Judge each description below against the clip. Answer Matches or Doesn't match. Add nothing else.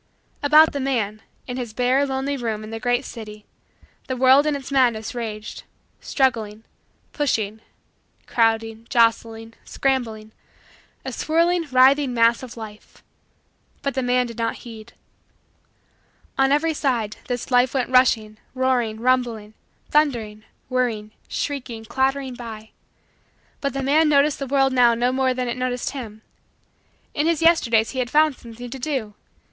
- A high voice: Matches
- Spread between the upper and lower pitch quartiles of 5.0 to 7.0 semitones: Doesn't match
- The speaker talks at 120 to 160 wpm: Matches